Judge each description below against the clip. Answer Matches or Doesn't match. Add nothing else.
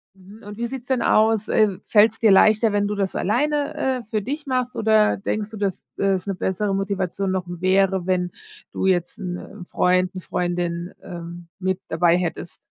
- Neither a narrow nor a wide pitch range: Matches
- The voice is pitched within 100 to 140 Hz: Doesn't match